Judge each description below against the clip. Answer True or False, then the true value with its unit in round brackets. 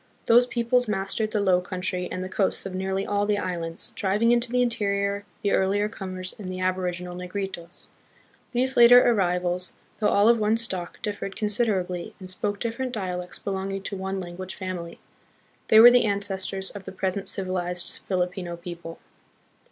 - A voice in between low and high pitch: False (195 Hz)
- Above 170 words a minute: False (165 wpm)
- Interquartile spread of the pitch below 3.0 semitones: True (2.5 semitones)